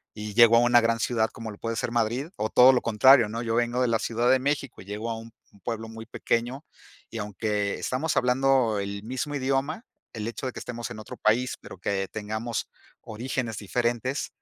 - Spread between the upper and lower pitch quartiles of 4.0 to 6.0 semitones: No, narrow, 2.5 semitones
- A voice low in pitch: Yes, low, 115 Hz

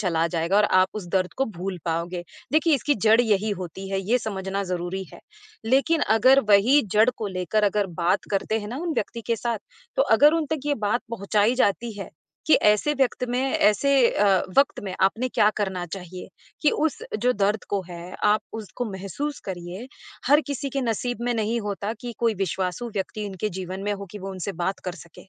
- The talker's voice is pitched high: Yes, high, 210 Hz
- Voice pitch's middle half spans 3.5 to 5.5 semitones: Yes, average, 4.3 semitones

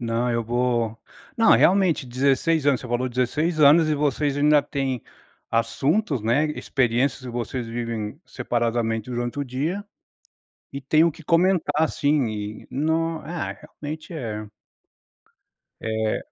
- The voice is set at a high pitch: No, low, 135 Hz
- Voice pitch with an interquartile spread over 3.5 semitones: Yes, average, 4.6 semitones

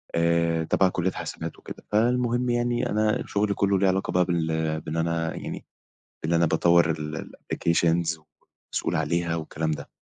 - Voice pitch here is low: Yes, very low, 85 Hz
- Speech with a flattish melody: No, average, 3.6 semitones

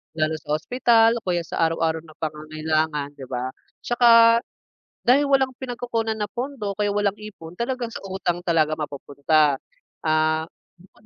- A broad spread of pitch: Yes, wide, 6.9 semitones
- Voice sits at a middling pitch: Yes, medium, 175 Hz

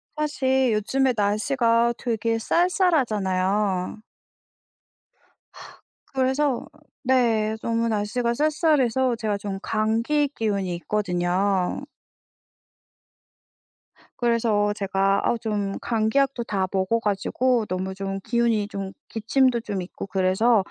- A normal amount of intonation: Yes, average, 3.9 semitones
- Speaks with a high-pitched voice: Yes, high, 220 Hz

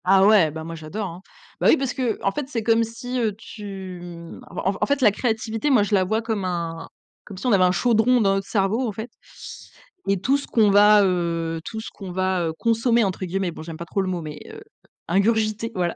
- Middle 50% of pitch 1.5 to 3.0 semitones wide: No, average, 3.9 semitones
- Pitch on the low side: No, high, 200 Hz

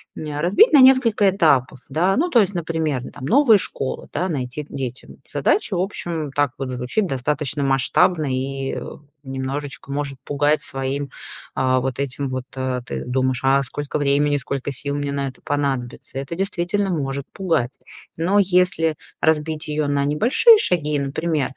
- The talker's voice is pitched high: No, medium, 145 Hz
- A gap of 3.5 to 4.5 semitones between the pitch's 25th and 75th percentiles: Yes, average, 4.2 semitones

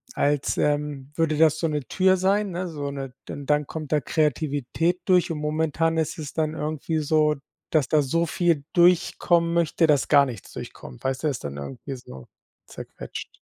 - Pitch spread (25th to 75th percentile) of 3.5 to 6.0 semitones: No, average, 2.7 semitones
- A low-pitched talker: No, medium, 155 Hz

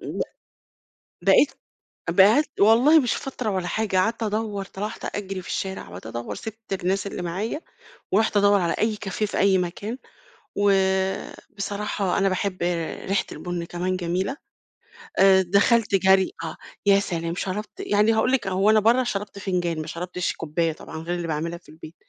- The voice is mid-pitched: No, high, 195 Hz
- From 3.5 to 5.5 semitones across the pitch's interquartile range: No, average, 3.0 semitones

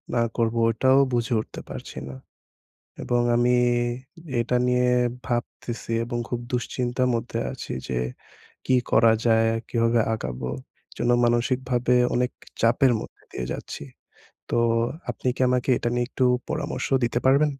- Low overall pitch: Yes, low, 120 Hz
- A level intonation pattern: Yes, narrow, 1.4 semitones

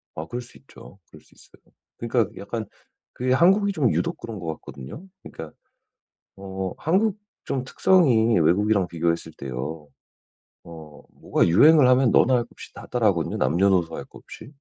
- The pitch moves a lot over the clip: Yes, wide, 7.4 semitones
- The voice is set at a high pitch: No, low, 105 Hz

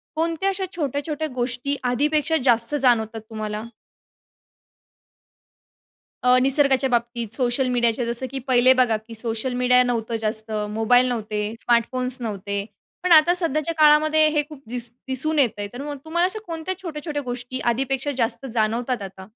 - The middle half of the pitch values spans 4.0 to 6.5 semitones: Yes, average, 4.4 semitones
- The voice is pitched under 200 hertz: No, very high, 250 Hz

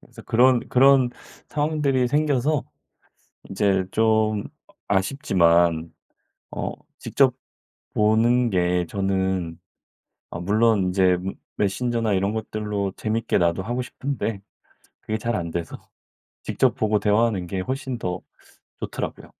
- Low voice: Yes, low, 105 Hz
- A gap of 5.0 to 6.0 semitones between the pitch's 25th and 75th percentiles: No, average, 4.6 semitones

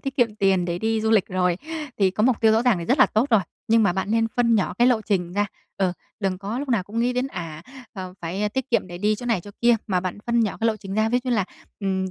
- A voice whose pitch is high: Yes, high, 210 Hz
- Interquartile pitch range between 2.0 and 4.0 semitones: Yes, average, 3.7 semitones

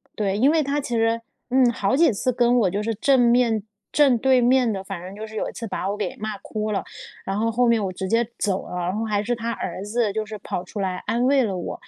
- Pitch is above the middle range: Yes, high, 220 Hz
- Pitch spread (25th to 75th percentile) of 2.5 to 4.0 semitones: Yes, average, 3.4 semitones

